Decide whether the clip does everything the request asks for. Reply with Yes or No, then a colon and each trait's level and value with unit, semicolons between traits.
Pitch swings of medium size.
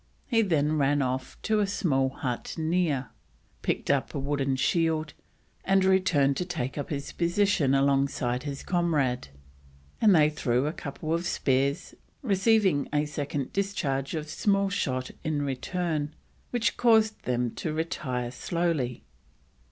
Yes: average, 4.7 semitones